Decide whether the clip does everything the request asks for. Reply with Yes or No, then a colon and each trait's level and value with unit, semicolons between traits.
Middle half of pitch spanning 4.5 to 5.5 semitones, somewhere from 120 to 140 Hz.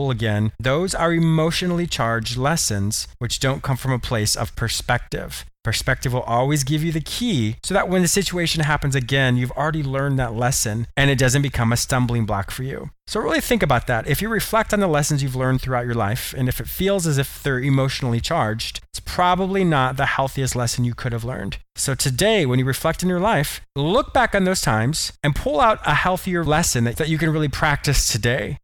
Yes: average, 5.1 semitones; low, 135 Hz